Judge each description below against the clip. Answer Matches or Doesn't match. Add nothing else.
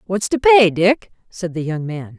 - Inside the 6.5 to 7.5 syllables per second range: Doesn't match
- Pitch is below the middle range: Doesn't match